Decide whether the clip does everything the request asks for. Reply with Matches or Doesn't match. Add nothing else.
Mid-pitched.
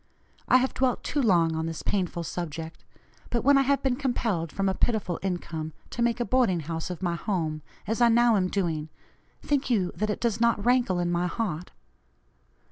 Doesn't match